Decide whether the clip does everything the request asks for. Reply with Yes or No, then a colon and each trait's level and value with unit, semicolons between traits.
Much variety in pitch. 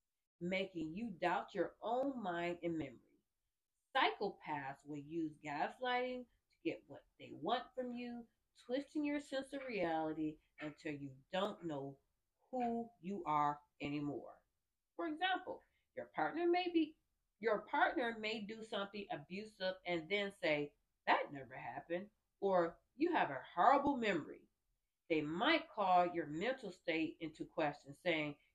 Yes: wide, 7.6 semitones